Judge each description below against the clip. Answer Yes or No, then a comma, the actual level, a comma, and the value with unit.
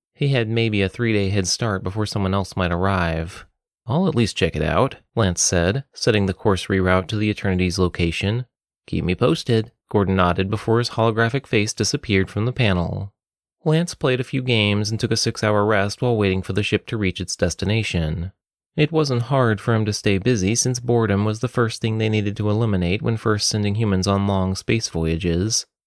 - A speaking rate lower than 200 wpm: No, fast, 205 wpm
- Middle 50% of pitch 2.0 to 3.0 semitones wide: No, average, 3.5 semitones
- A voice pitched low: Yes, low, 105 Hz